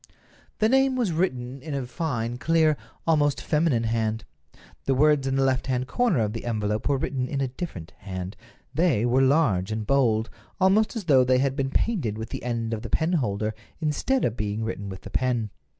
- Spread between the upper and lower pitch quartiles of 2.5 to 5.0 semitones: No, wide, 5.5 semitones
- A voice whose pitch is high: No, low, 130 Hz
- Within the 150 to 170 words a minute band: No, average, 200 wpm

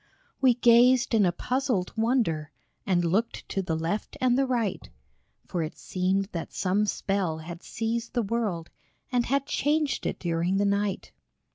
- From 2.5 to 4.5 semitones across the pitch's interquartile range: No, wide, 5.4 semitones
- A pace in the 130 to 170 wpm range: Yes, average, 160 wpm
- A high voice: Yes, high, 205 Hz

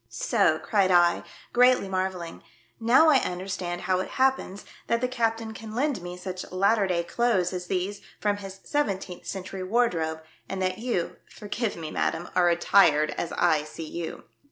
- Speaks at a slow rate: No, average, 180 wpm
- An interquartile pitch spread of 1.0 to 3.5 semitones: No, average, 4.2 semitones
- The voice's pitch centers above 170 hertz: Yes, high, 190 Hz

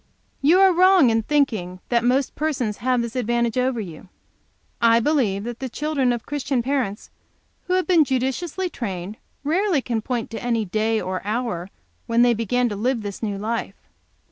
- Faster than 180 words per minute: No, average, 175 wpm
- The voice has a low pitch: No, high, 240 Hz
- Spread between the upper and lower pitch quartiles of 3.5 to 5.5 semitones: Yes, average, 4.2 semitones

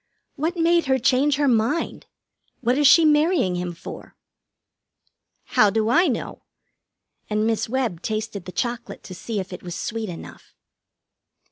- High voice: Yes, high, 230 Hz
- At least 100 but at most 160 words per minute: Yes, average, 150 wpm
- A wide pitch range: Yes, wide, 5.8 semitones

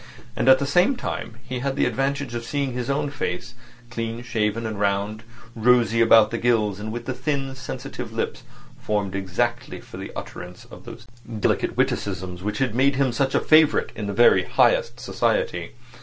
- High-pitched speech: No, low, 120 Hz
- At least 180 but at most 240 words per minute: Yes, average, 185 wpm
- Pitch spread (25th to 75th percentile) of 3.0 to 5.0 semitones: Yes, average, 4.3 semitones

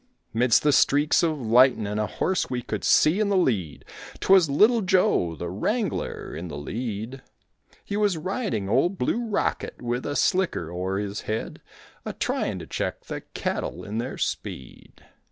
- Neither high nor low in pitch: No, low, 130 Hz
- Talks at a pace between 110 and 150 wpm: No, average, 165 wpm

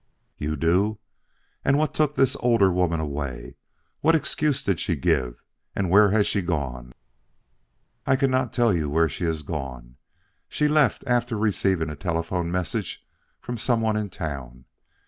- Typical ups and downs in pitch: No, wide, 8.0 semitones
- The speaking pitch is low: Yes, very low, 90 Hz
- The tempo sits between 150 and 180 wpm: Yes, average, 155 wpm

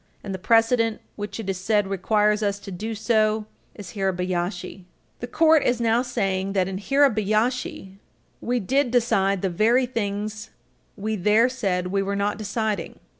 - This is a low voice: No, high, 210 Hz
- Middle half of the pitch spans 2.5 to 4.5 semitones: Yes, average, 2.8 semitones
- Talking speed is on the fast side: No, average, 160 wpm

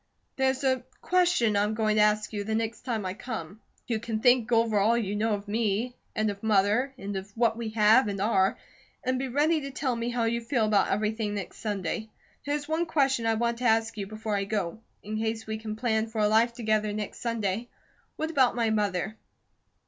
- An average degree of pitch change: No, narrow, 2.3 semitones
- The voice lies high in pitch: Yes, high, 220 Hz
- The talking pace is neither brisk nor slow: No, fast, 215 wpm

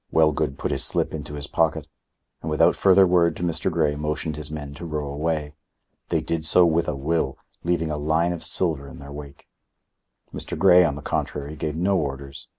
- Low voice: Yes, very low, 75 Hz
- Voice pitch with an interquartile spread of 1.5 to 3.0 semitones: Yes, narrow, 2.4 semitones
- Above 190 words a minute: Yes, average, 200 wpm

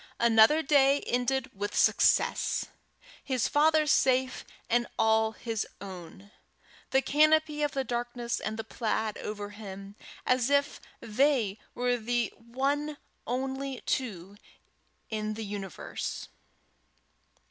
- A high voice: Yes, high, 240 Hz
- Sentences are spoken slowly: Yes, slow, 110 wpm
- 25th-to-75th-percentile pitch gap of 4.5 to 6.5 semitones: No, average, 4.0 semitones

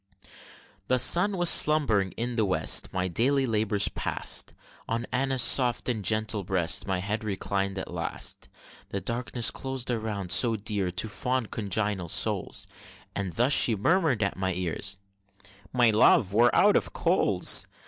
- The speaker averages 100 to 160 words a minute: Yes, average, 150 wpm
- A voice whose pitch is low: Yes, low, 110 Hz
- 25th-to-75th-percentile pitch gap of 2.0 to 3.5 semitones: No, average, 4.2 semitones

